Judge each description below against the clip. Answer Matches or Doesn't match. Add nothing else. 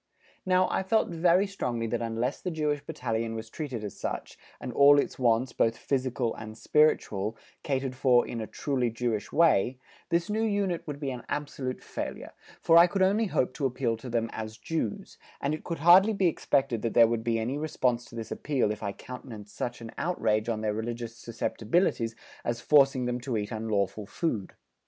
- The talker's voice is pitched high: Doesn't match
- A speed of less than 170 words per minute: Doesn't match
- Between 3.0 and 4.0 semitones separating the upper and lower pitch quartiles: Doesn't match